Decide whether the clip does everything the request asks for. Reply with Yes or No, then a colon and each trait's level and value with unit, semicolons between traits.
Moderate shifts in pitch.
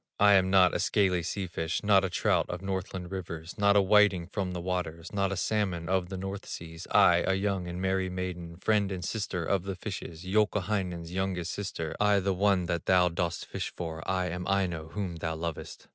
No: narrow, 2.2 semitones